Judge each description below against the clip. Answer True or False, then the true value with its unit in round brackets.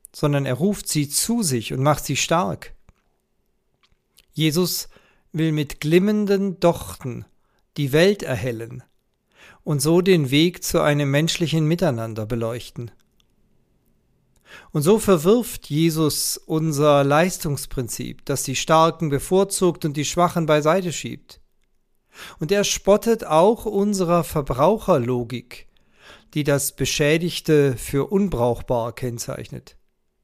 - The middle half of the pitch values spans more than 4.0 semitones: True (5.0 semitones)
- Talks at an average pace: False (105 wpm)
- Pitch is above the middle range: False (155 Hz)